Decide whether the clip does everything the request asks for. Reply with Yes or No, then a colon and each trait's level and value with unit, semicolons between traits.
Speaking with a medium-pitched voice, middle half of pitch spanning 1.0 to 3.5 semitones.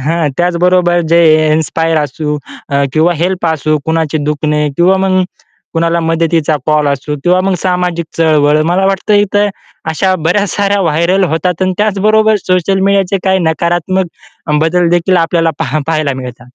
Yes: medium, 170 Hz; average, 3.0 semitones